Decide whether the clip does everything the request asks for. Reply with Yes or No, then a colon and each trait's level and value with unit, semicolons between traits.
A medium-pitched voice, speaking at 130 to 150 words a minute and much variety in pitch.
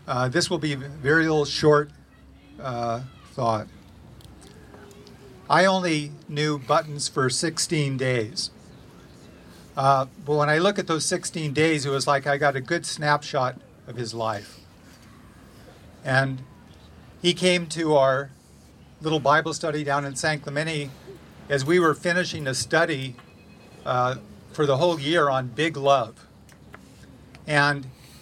No: medium, 145 Hz; slow, 135 wpm; average, 3.8 semitones